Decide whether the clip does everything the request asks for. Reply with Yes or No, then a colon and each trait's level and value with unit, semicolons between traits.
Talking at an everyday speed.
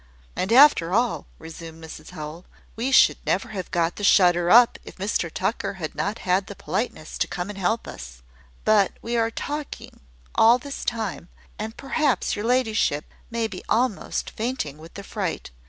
Yes: average, 170 wpm